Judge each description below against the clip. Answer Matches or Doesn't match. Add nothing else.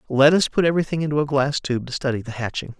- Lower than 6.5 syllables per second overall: Doesn't match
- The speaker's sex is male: Matches